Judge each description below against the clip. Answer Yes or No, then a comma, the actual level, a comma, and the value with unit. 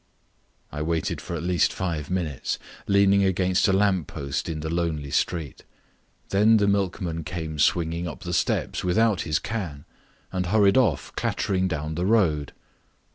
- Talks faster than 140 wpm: Yes, average, 155 wpm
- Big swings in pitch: No, average, 3.9 semitones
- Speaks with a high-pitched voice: No, very low, 90 Hz